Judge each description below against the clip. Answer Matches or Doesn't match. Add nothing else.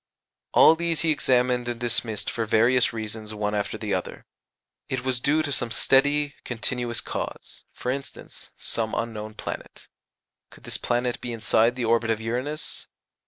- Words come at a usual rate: Matches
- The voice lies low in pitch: Matches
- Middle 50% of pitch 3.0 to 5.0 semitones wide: Doesn't match